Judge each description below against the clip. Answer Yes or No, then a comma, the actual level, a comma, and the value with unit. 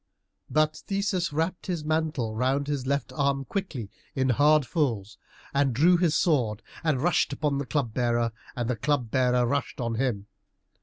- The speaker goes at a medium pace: Yes, average, 165 wpm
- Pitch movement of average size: Yes, average, 4.0 semitones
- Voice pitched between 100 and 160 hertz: Yes, medium, 140 Hz